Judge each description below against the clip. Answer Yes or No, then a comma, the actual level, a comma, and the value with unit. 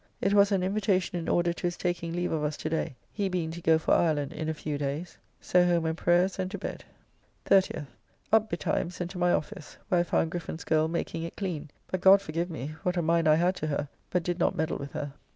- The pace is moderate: No, fast, 245 wpm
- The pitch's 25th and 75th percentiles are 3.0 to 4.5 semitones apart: No, narrow, 2.4 semitones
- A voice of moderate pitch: Yes, medium, 170 Hz